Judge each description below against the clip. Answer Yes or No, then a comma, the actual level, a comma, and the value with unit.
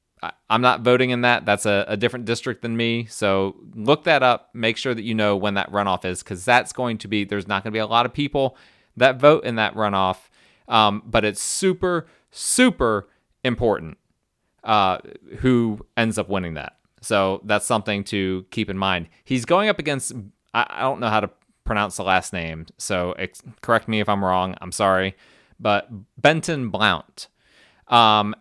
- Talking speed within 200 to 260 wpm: No, average, 190 wpm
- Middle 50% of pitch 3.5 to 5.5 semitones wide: Yes, average, 3.8 semitones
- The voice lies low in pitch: Yes, low, 110 Hz